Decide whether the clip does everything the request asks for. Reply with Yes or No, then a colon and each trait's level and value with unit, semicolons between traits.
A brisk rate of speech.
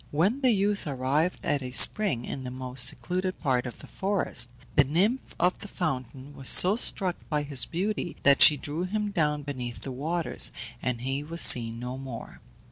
No: average, 190 wpm